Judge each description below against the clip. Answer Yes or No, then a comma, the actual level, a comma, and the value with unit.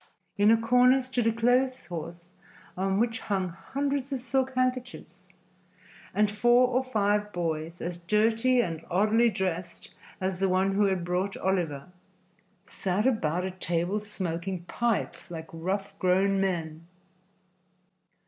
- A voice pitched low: No, high, 195 Hz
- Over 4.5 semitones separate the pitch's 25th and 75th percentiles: Yes, average, 4.9 semitones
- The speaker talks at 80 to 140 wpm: Yes, slow, 135 wpm